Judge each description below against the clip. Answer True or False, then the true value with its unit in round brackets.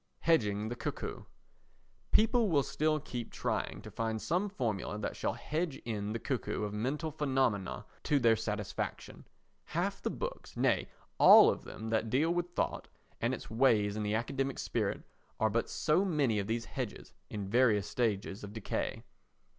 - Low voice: True (115 Hz)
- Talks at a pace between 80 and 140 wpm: False (160 wpm)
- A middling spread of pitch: False (5.7 semitones)